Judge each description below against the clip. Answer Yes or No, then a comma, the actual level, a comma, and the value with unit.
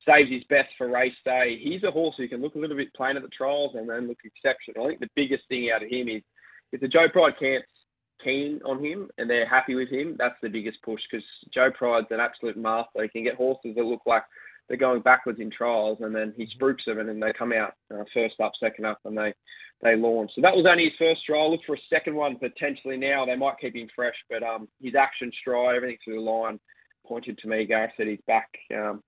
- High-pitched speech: No, low, 125 Hz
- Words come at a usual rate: No, fast, 250 wpm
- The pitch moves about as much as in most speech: Yes, average, 3.3 semitones